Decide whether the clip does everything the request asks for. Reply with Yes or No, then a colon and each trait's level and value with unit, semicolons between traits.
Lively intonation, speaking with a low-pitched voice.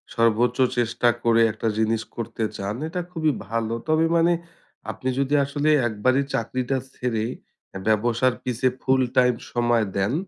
No: average, 2.7 semitones; low, 120 Hz